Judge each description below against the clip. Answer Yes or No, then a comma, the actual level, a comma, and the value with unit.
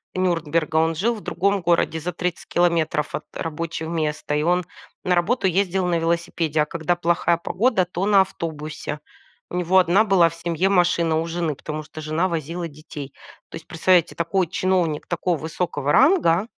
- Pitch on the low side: No, medium, 170 Hz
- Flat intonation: Yes, narrow, 2.3 semitones